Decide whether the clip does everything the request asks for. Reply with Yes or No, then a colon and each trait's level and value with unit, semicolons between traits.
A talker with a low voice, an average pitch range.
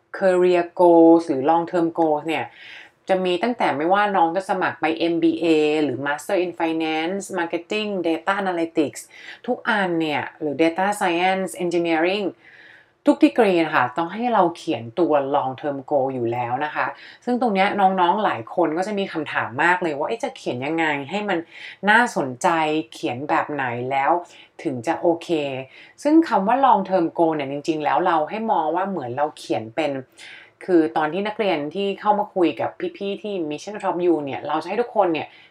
No: medium, 170 Hz; average, 3.9 semitones